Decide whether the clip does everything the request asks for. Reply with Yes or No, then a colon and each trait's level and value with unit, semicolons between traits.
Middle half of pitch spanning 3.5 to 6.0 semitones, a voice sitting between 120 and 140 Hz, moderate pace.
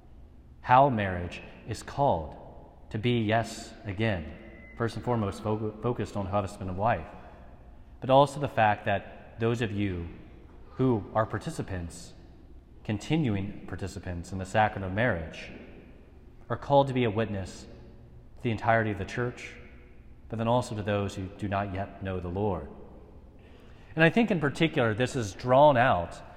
No: average, 4.8 semitones; low, 105 Hz; average, 155 wpm